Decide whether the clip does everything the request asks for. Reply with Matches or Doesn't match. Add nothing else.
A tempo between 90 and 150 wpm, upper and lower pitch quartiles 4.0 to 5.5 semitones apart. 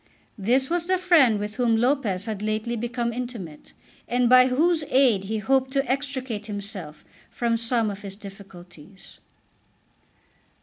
Matches